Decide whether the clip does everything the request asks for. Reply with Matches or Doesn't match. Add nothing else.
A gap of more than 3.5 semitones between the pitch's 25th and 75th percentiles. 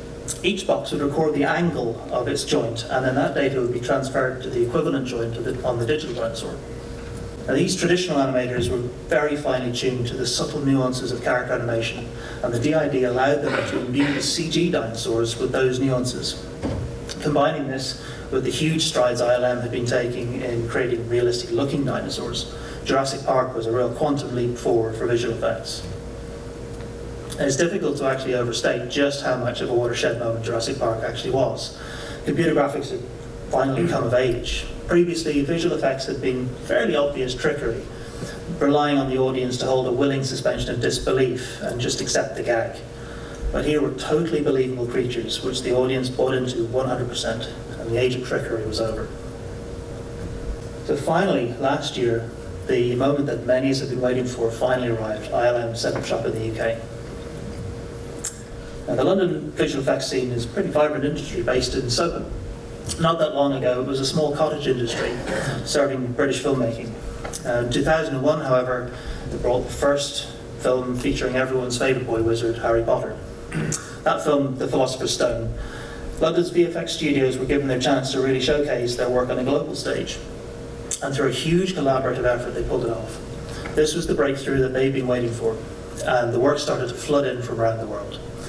Doesn't match